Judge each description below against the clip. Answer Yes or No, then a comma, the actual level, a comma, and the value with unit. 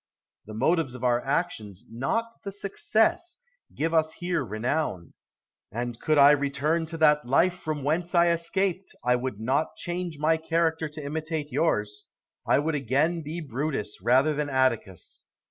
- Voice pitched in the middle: Yes, medium, 150 Hz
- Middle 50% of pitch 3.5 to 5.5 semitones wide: Yes, average, 4.6 semitones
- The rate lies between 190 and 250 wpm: No, average, 160 wpm